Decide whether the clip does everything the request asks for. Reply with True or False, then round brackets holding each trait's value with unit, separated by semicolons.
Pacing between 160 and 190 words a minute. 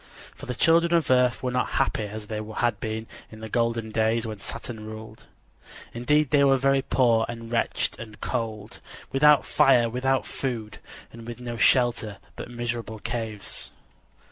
True (165 wpm)